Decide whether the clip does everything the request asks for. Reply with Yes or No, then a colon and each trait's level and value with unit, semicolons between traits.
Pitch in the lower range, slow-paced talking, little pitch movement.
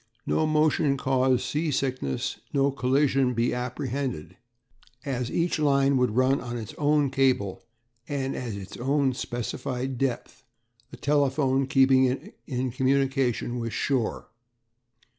Yes: low, 130 Hz; slow, 125 wpm; narrow, 1.9 semitones